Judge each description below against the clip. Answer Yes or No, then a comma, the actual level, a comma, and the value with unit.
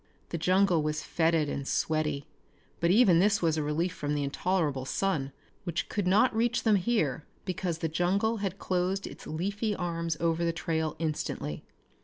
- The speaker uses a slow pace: No, average, 170 wpm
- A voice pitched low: No, medium, 170 Hz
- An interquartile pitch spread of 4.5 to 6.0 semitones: No, average, 3.8 semitones